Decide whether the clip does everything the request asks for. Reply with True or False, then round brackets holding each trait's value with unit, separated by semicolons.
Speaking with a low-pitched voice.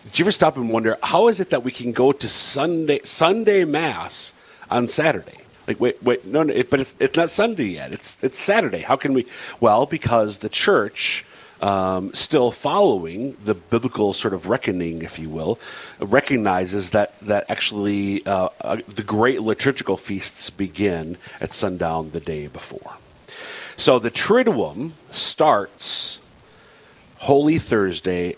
True (110 Hz)